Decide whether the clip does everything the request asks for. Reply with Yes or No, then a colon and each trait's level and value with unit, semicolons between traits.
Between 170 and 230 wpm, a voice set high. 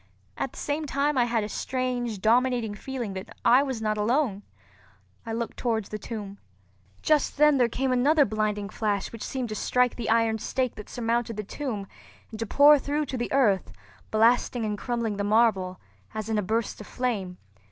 Yes: average, 190 wpm; high, 230 Hz